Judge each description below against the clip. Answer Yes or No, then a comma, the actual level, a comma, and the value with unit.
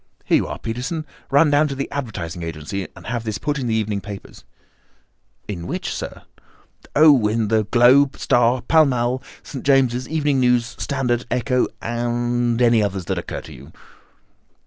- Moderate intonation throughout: Yes, average, 3.7 semitones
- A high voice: No, low, 120 Hz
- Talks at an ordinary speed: Yes, average, 170 wpm